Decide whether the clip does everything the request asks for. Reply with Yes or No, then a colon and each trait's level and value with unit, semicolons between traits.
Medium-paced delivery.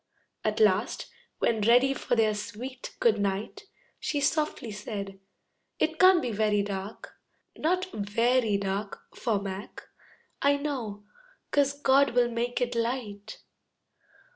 No: slow, 125 wpm